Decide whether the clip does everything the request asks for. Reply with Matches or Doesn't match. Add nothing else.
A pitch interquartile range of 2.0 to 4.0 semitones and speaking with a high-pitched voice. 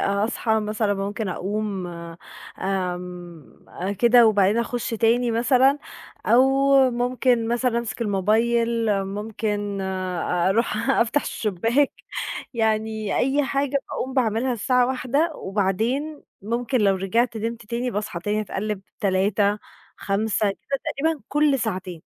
Matches